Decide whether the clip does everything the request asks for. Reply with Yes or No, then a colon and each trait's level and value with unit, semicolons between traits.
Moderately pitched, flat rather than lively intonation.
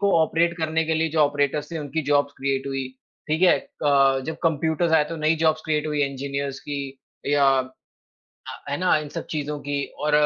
Yes: medium, 150 Hz; narrow, 2.2 semitones